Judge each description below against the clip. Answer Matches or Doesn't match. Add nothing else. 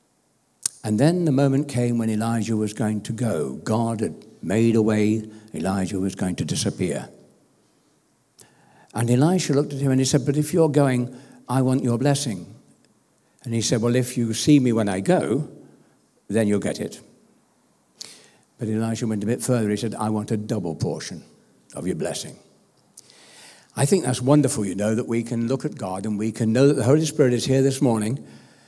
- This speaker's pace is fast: Doesn't match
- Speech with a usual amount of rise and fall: Matches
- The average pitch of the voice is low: Matches